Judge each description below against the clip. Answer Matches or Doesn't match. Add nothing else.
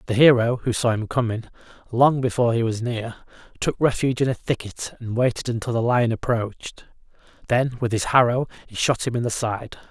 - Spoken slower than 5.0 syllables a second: Doesn't match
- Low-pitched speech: Matches